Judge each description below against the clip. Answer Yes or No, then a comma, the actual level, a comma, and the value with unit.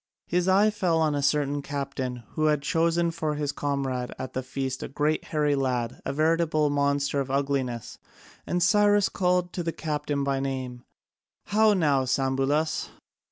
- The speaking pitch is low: No, medium, 145 Hz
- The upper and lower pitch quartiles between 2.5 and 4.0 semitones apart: Yes, average, 3.4 semitones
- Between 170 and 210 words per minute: No, average, 160 wpm